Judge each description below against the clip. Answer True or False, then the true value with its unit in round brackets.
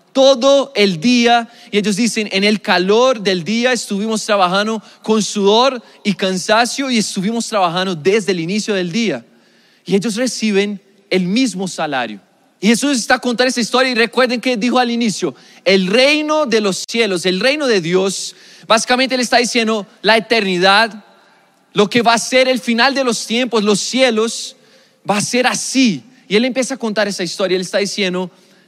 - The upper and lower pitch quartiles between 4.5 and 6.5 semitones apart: False (4.0 semitones)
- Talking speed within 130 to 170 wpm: False (180 wpm)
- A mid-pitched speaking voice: False (220 Hz)